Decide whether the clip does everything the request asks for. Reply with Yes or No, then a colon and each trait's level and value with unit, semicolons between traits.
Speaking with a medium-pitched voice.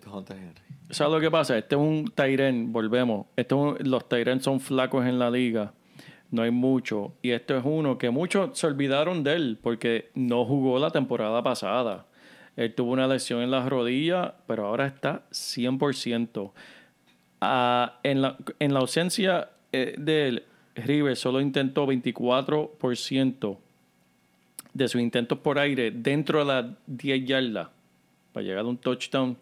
No: low, 130 Hz